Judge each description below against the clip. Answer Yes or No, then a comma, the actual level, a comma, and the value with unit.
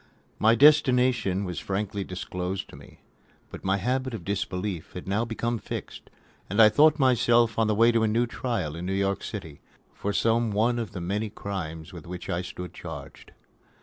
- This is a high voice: No, low, 105 Hz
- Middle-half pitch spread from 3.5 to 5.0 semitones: Yes, average, 4.2 semitones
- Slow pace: No, average, 180 wpm